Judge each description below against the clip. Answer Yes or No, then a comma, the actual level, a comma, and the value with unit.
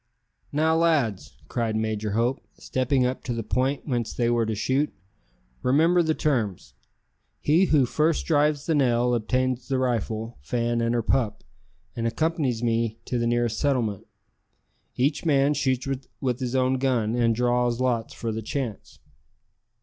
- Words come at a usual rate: Yes, average, 155 wpm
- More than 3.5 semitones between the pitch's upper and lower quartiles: No, average, 3.2 semitones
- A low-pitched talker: Yes, low, 125 Hz